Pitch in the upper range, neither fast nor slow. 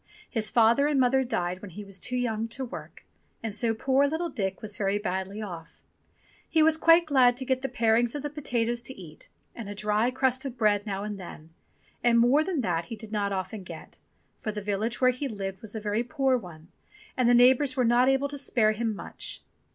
No: high, 230 Hz; fast, 220 wpm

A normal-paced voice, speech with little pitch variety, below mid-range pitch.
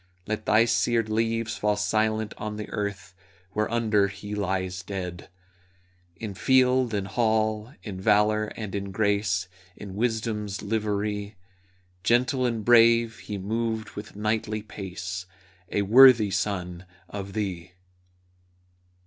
No: slow, 120 wpm; narrow, 2.1 semitones; low, 105 Hz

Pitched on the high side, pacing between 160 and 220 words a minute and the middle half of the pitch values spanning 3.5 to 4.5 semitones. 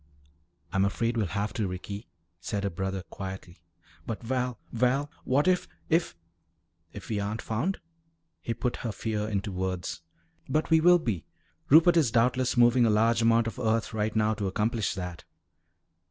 No: low, 110 Hz; average, 170 wpm; average, 4.0 semitones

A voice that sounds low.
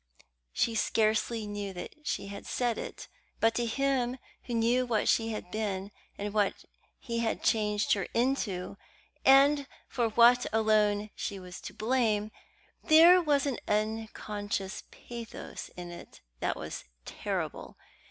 No: high, 220 Hz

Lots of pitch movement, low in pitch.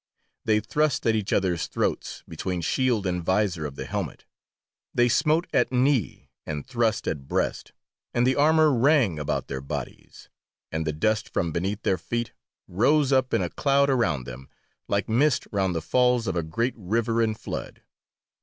Yes: wide, 6.5 semitones; low, 110 Hz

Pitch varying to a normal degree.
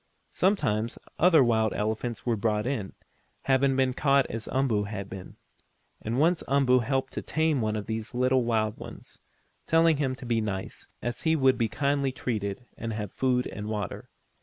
Yes: average, 4.0 semitones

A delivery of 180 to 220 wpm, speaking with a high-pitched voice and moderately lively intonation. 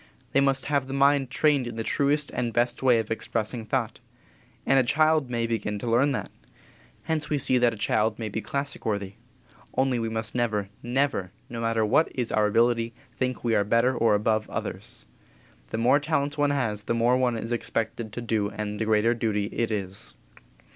No: average, 200 wpm; low, 120 Hz; average, 3.4 semitones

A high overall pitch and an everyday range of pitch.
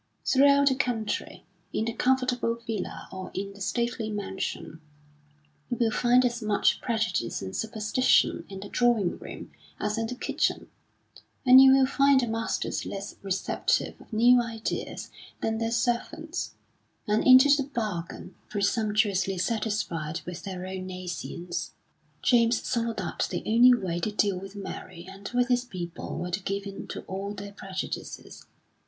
Yes: high, 215 Hz; average, 4.1 semitones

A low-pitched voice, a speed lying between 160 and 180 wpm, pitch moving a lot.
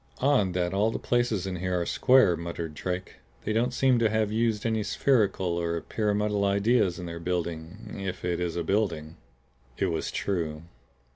No: very low, 95 Hz; average, 175 wpm; average, 4.2 semitones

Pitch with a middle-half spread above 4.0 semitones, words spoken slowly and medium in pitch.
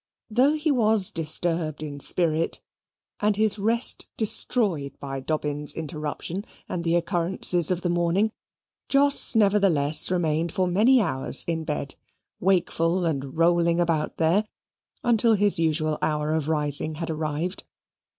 Yes: average, 4.4 semitones; slow, 130 wpm; medium, 170 Hz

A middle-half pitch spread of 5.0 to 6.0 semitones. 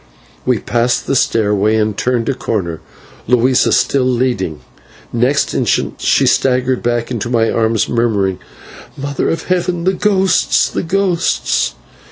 No: average, 3.7 semitones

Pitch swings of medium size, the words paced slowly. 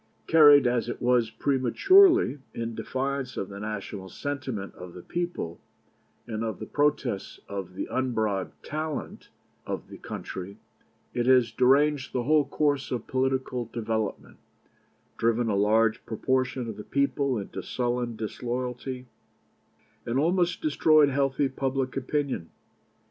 Yes: average, 3.9 semitones; slow, 130 wpm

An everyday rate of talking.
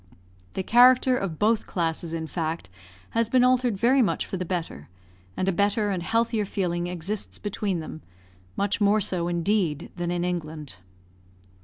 Yes: average, 160 wpm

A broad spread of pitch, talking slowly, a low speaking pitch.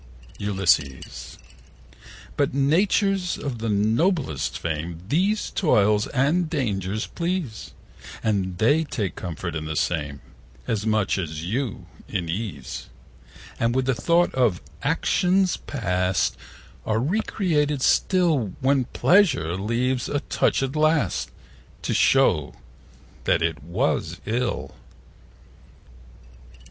Yes: wide, 8.6 semitones; slow, 110 wpm; low, 115 Hz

